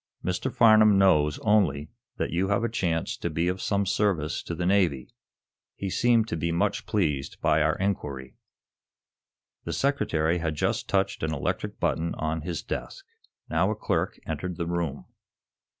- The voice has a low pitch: Yes, very low, 85 Hz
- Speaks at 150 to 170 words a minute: Yes, average, 165 wpm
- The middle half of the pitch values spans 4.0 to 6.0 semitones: Yes, average, 4.3 semitones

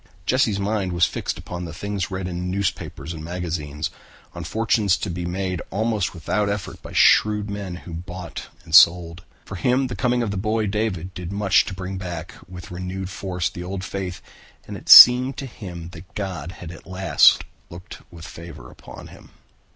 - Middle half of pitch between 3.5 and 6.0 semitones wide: No, average, 2.8 semitones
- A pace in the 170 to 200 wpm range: Yes, average, 185 wpm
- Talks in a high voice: No, very low, 90 Hz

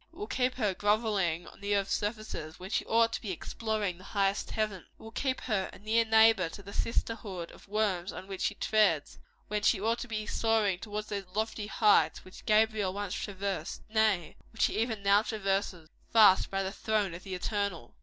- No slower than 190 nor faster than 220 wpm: Yes, fast, 205 wpm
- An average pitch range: No, narrow, 2.3 semitones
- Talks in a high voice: Yes, high, 205 Hz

